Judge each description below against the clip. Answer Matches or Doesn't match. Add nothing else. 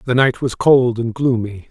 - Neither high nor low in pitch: Doesn't match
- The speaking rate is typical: Doesn't match